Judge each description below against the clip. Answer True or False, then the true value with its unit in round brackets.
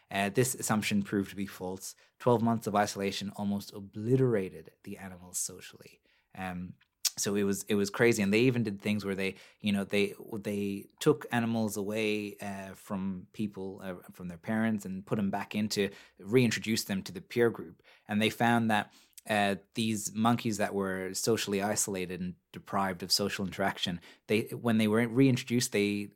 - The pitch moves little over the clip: True (2.2 semitones)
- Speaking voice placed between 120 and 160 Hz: False (105 Hz)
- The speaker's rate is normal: True (175 wpm)